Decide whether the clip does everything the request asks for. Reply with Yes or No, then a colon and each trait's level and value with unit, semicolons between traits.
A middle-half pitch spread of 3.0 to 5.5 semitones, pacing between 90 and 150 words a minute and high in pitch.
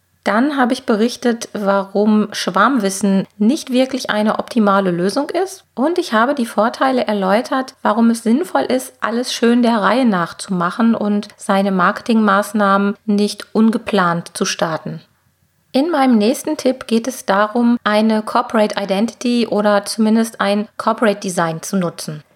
Yes: average, 3.3 semitones; average, 140 wpm; high, 220 Hz